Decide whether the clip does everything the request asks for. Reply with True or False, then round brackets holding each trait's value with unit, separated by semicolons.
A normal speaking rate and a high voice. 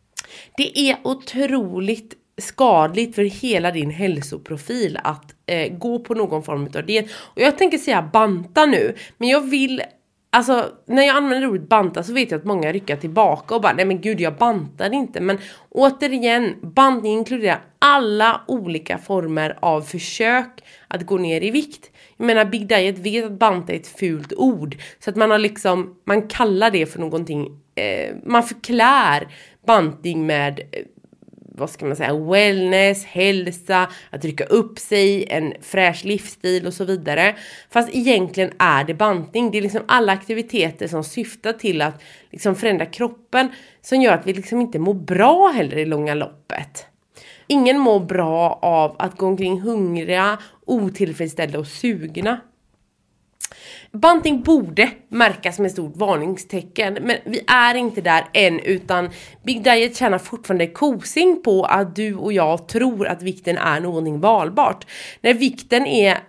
True (160 wpm; 205 Hz)